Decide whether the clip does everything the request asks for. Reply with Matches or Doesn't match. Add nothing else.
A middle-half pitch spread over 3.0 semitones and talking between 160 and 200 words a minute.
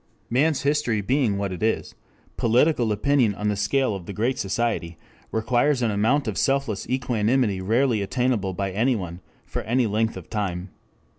Matches